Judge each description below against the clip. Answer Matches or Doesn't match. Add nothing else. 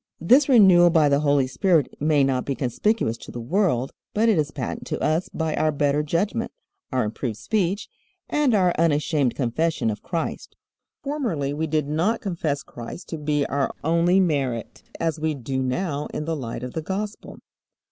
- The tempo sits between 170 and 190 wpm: Matches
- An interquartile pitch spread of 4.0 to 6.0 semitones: Matches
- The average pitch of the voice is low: Doesn't match